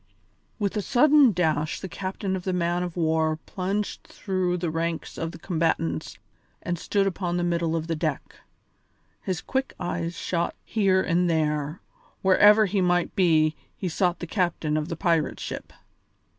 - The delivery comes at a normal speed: Yes, average, 165 wpm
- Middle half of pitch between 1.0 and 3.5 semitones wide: Yes, average, 2.7 semitones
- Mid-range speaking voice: Yes, medium, 175 Hz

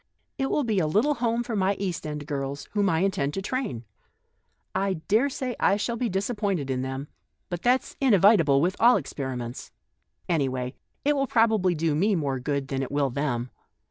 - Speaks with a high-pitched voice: No, medium, 180 Hz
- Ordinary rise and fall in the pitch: No, wide, 8.0 semitones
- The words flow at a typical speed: Yes, average, 185 wpm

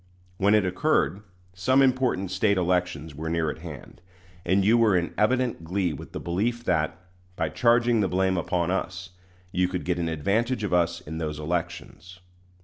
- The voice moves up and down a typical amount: Yes, average, 3.7 semitones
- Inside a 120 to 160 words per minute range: No, average, 175 wpm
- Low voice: Yes, very low, 90 Hz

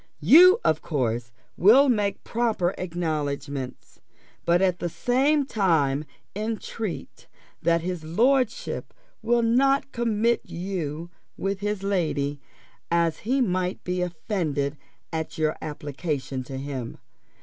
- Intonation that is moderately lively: No, wide, 6.6 semitones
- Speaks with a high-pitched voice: No, medium, 180 Hz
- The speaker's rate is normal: No, slow, 115 wpm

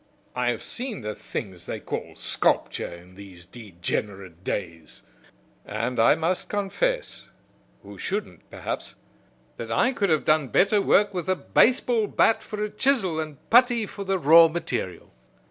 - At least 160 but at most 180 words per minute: No, average, 150 wpm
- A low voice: No, medium, 160 Hz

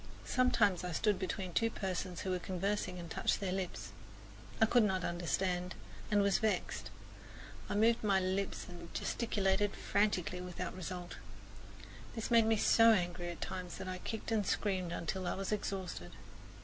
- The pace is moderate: Yes, average, 160 wpm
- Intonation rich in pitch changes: No, narrow, 2.5 semitones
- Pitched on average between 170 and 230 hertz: Yes, high, 190 Hz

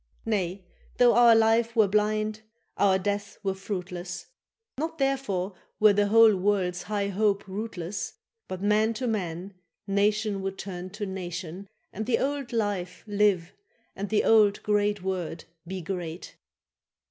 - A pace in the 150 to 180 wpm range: No, average, 140 wpm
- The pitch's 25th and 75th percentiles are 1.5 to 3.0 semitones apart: Yes, narrow, 2.4 semitones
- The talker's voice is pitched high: Yes, high, 205 Hz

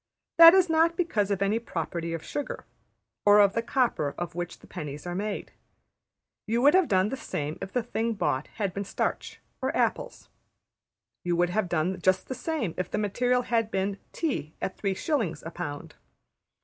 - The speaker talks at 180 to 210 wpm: Yes, average, 185 wpm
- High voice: Yes, high, 200 Hz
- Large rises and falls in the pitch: Yes, wide, 5.7 semitones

